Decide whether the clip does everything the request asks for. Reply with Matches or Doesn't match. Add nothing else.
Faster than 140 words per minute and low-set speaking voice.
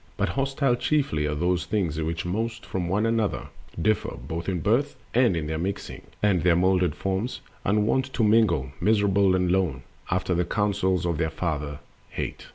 Matches